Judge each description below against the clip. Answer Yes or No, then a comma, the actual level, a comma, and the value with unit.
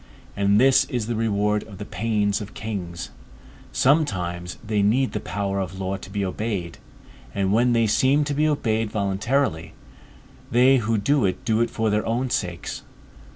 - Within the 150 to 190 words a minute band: Yes, average, 170 wpm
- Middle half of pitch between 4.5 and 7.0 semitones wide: No, average, 3.4 semitones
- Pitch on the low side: Yes, low, 105 Hz